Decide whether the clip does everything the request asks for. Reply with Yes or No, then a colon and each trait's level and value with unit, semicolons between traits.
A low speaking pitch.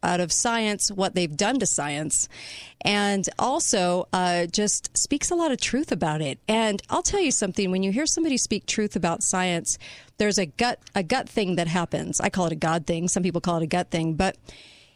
No: high, 195 Hz